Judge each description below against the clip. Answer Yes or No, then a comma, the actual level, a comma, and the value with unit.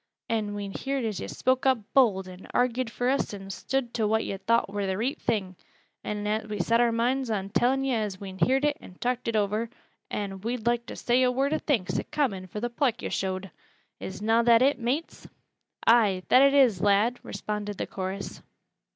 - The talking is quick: Yes, fast, 210 wpm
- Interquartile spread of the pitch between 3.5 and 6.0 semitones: Yes, average, 3.9 semitones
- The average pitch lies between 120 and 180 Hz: No, high, 225 Hz